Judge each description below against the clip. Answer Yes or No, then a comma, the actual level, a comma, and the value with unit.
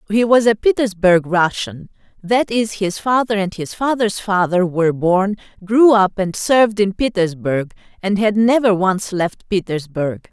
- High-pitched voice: Yes, high, 200 Hz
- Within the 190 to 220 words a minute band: No, average, 155 wpm